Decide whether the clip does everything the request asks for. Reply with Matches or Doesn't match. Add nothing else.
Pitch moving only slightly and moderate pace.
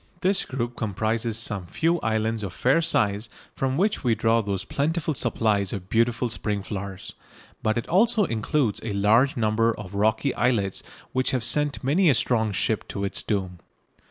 Doesn't match